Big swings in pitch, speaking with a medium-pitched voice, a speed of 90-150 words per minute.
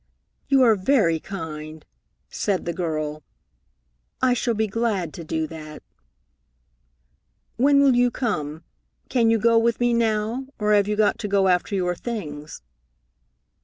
No: wide, 6.2 semitones; high, 205 Hz; average, 145 wpm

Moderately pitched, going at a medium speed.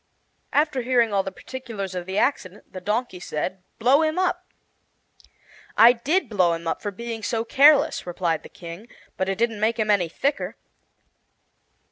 No: high, 220 Hz; average, 165 wpm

